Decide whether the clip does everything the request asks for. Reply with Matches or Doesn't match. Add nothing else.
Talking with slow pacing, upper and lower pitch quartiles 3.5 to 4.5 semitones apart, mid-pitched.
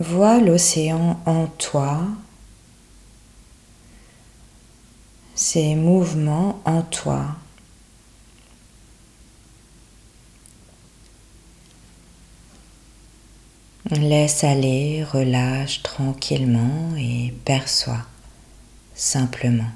Matches